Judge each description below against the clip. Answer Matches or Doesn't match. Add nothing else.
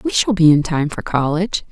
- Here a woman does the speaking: Matches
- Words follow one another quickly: Matches